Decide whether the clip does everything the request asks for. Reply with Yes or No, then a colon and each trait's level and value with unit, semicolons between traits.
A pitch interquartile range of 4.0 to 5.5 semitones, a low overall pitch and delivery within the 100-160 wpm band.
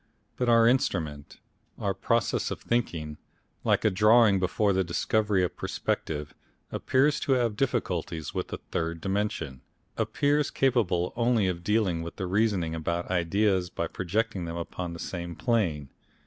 Yes: average, 5.1 semitones; very low, 95 Hz; average, 150 wpm